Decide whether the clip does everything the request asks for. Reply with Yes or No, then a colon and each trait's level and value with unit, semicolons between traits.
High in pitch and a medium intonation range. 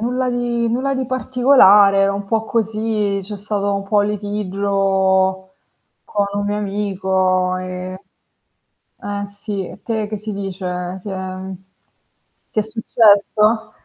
No: high, 205 Hz; narrow, 2.3 semitones